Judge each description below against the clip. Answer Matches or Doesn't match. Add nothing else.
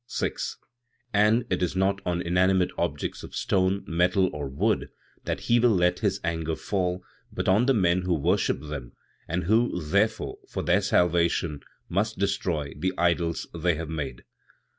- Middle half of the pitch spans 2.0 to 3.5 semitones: Matches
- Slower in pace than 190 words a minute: Matches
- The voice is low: Matches